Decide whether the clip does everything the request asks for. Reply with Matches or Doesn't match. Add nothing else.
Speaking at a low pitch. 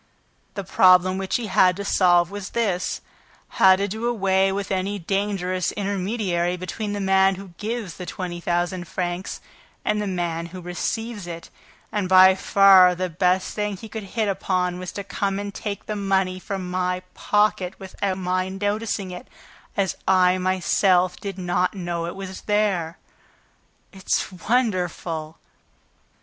Doesn't match